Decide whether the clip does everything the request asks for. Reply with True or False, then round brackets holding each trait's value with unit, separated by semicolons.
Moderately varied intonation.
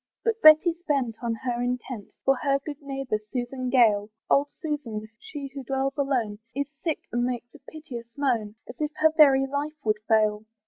True (3.6 semitones)